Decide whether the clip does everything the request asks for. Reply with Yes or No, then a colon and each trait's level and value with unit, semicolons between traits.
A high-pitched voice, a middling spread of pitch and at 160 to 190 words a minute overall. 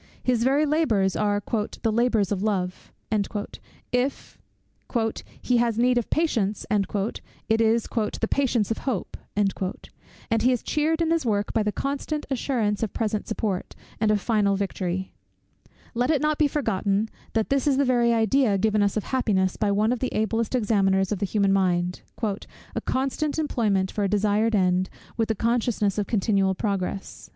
Yes: high, 220 Hz; average, 3.7 semitones; average, 165 wpm